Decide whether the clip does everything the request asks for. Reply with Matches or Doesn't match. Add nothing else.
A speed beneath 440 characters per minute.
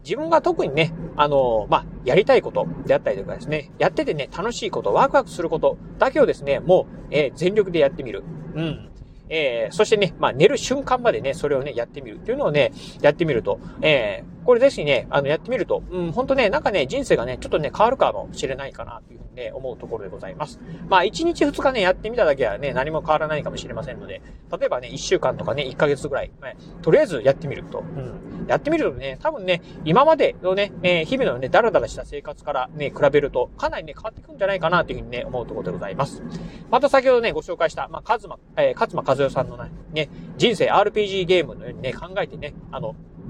Doesn't match